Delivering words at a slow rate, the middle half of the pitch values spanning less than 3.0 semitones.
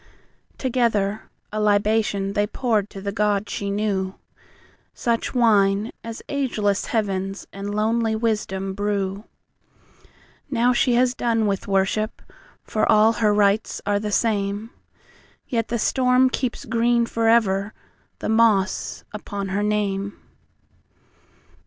Yes: slow, 100 wpm; narrow, 2.5 semitones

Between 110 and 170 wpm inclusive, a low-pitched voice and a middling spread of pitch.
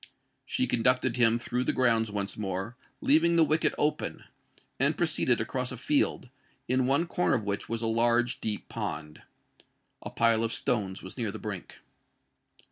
Yes: average, 160 wpm; low, 115 Hz; average, 3.2 semitones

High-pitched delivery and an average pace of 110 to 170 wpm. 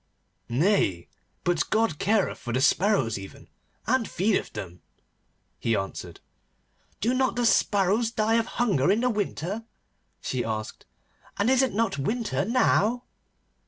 Yes: high, 205 Hz; slow, 135 wpm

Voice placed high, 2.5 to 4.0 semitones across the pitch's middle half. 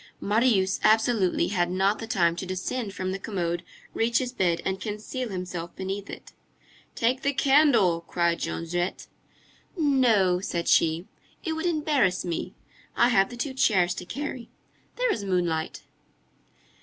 No: high, 195 Hz; wide, 5.5 semitones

